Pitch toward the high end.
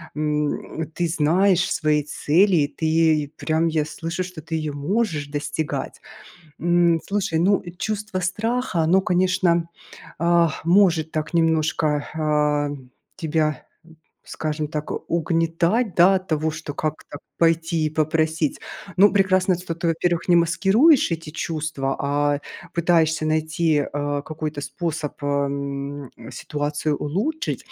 No: medium, 160 Hz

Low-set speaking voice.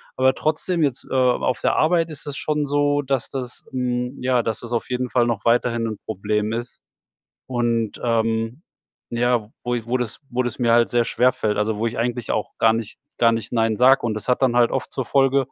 Yes: low, 120 Hz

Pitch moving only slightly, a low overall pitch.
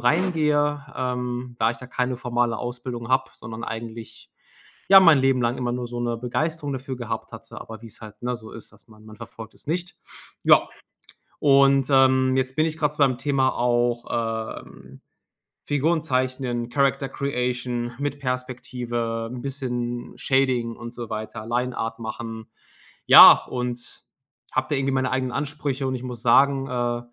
Yes: narrow, 2.3 semitones; low, 125 Hz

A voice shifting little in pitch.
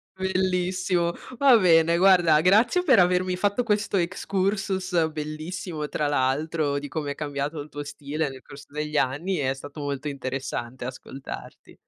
No: average, 4.4 semitones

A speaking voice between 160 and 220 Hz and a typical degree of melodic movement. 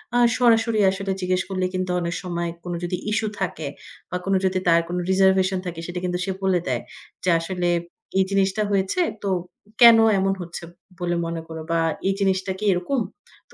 No: medium, 185 Hz; narrow, 1.8 semitones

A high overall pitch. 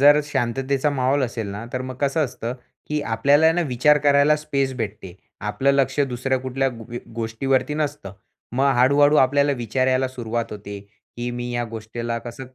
No: low, 130 Hz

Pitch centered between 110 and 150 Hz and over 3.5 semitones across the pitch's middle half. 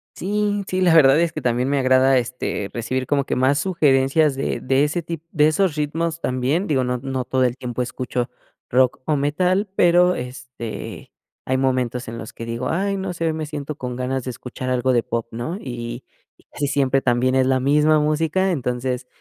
Yes: low, 135 Hz; average, 3.9 semitones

